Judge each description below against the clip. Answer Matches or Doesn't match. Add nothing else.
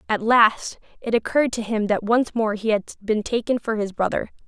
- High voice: Matches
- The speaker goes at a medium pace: Doesn't match